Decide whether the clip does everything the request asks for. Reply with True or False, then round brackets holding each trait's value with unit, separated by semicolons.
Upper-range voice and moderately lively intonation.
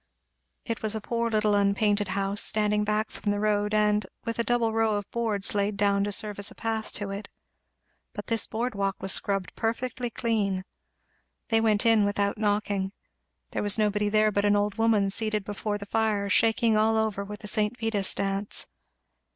False (210 Hz; 1.6 semitones)